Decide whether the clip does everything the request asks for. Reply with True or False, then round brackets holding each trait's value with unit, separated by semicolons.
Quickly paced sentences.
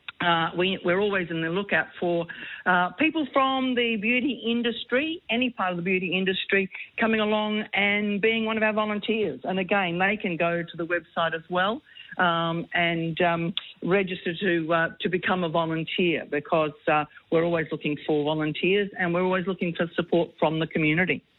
False (180 wpm)